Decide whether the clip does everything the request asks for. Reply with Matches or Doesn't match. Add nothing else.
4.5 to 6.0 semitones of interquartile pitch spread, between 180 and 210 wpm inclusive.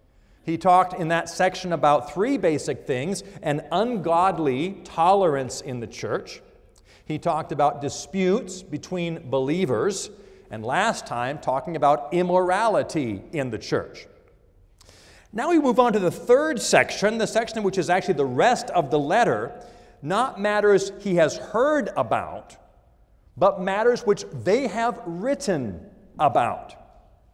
Doesn't match